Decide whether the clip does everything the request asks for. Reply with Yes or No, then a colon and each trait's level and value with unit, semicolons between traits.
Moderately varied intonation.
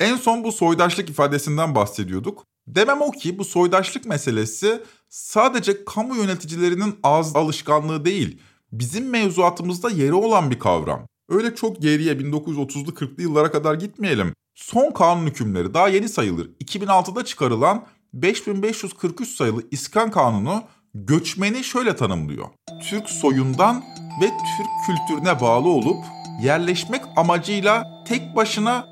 No: wide, 6.0 semitones